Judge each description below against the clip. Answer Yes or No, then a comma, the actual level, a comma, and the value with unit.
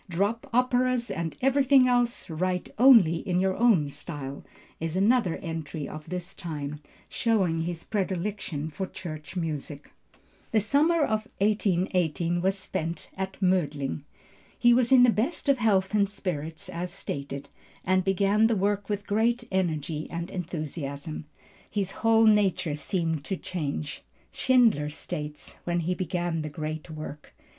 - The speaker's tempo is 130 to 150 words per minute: Yes, average, 140 wpm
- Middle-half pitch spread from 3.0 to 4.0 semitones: No, average, 5.1 semitones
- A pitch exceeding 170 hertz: Yes, medium, 185 Hz